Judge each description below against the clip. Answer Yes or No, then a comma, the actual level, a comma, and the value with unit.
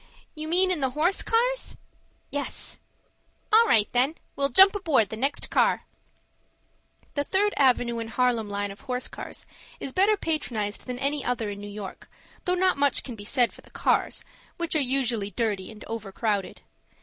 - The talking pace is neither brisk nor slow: Yes, average, 175 wpm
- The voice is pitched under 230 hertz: No, very high, 255 Hz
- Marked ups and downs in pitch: Yes, wide, 6.5 semitones